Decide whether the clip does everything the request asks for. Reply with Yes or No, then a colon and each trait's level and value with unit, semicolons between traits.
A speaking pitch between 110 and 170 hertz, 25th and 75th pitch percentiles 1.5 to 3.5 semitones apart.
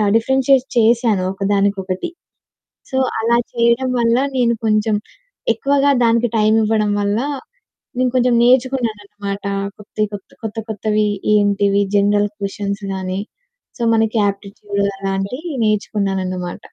No: high, 215 Hz; average, 2.7 semitones